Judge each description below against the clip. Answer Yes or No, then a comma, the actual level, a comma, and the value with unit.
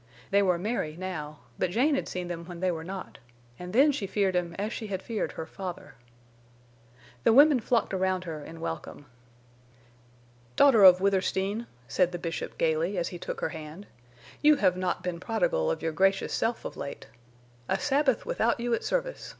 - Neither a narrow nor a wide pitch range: Yes, average, 4.9 semitones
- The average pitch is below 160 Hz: No, high, 190 Hz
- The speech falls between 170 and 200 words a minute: Yes, average, 185 wpm